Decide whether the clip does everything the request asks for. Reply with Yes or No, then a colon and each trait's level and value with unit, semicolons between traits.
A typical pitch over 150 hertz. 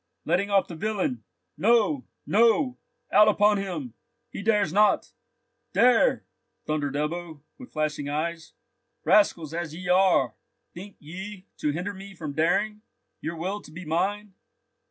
Yes: medium, 185 Hz